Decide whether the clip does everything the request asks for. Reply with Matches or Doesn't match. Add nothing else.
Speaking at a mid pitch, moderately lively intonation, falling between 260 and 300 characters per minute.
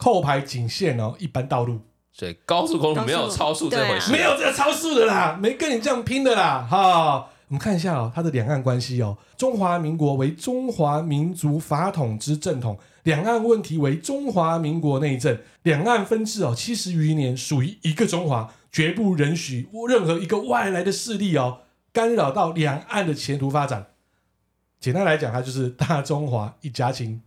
Doesn't match